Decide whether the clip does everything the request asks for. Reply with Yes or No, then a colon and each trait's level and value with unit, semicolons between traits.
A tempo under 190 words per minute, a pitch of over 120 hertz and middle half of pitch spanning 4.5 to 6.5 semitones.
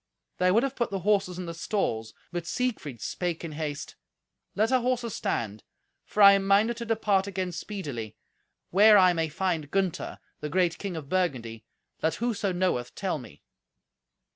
Yes: average, 170 wpm; medium, 185 Hz; average, 4.9 semitones